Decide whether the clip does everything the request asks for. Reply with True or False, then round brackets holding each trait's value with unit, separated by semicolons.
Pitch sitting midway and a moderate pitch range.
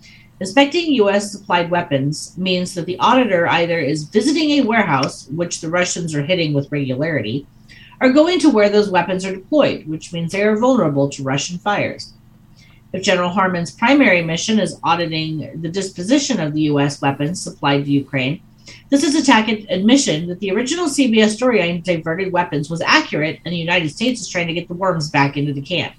False (175 Hz; 6.1 semitones)